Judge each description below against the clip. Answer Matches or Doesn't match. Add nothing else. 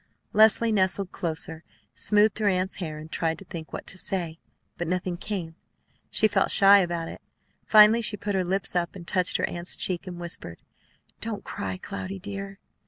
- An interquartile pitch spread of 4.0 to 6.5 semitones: Doesn't match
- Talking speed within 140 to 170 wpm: Doesn't match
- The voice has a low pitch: Doesn't match